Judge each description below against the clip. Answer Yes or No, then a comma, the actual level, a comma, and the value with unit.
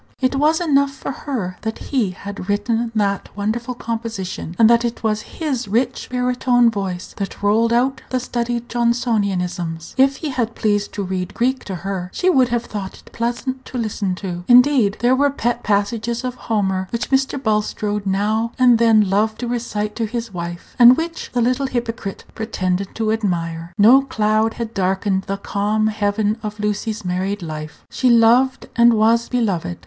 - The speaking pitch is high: Yes, high, 225 Hz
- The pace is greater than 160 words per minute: Yes, average, 175 wpm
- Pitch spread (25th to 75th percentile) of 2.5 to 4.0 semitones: Yes, average, 3.4 semitones